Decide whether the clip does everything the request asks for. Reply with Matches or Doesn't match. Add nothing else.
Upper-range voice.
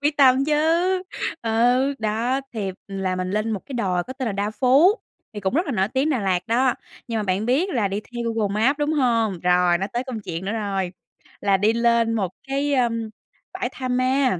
Matches